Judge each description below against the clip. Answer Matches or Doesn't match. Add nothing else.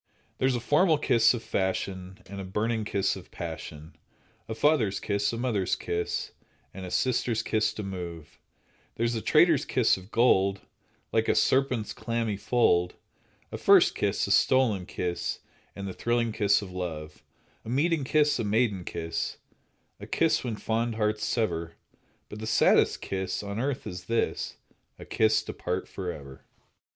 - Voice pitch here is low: Matches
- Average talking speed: Matches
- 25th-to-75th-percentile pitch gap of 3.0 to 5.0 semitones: Matches